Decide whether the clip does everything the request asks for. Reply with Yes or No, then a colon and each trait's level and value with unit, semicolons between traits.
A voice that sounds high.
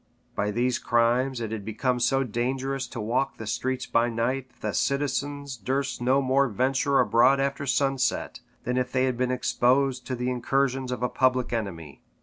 No: low, 125 Hz